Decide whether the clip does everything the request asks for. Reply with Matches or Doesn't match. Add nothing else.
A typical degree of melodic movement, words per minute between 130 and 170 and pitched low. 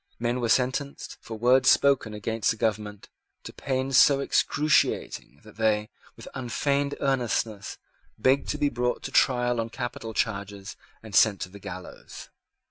Matches